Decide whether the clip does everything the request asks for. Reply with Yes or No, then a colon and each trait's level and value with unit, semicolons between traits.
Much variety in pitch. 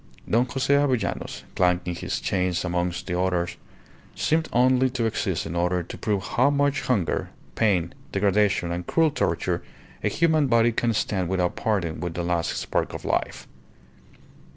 Yes: wide, 6.1 semitones